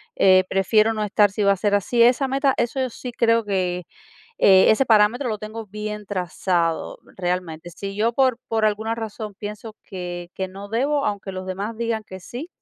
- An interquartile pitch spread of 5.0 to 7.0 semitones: No, average, 3.3 semitones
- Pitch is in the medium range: No, high, 210 Hz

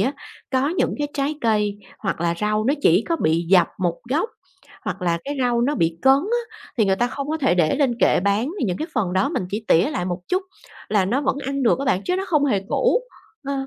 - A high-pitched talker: Yes, high, 235 Hz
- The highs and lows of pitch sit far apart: Yes, wide, 7.1 semitones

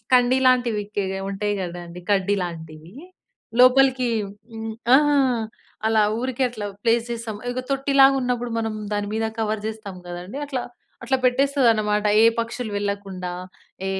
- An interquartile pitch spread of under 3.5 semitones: No, average, 3.8 semitones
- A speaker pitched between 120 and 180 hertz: No, high, 225 Hz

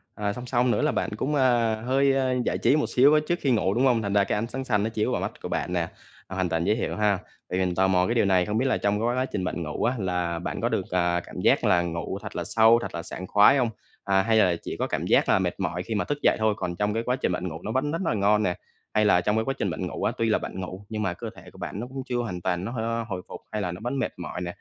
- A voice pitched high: No, low, 105 Hz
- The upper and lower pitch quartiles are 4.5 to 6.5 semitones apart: Yes, average, 4.8 semitones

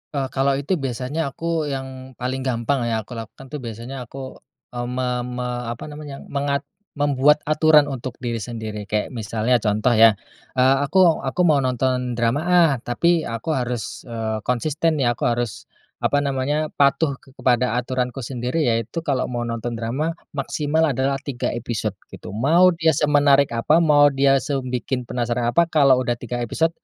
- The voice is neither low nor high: No, low, 130 Hz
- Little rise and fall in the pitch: No, average, 3.4 semitones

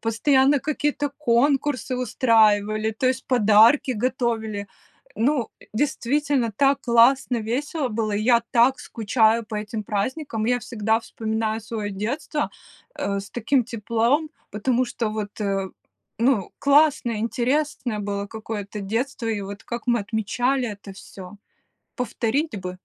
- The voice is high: Yes, high, 230 Hz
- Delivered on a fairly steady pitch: No, average, 3.5 semitones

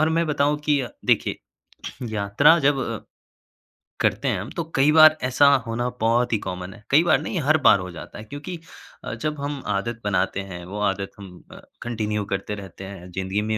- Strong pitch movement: Yes, wide, 6.6 semitones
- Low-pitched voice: Yes, low, 115 Hz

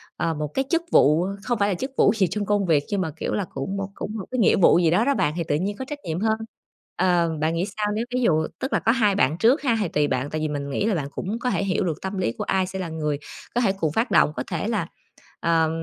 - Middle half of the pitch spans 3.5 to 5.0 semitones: No, wide, 5.4 semitones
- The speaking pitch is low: No, medium, 185 Hz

